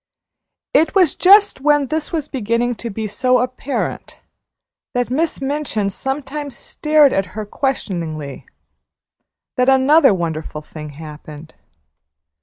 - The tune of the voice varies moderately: No, wide, 7.1 semitones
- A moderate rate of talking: No, slow, 115 wpm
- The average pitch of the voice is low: No, very high, 250 Hz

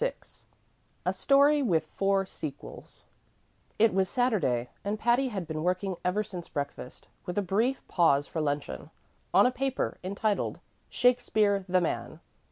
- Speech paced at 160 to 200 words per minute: No, average, 145 wpm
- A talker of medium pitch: No, high, 195 Hz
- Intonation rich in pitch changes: Yes, wide, 5.8 semitones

